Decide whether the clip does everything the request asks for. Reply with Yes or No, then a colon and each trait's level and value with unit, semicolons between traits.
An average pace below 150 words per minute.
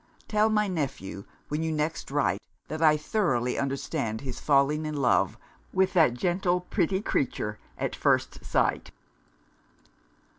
Yes: slow, 135 wpm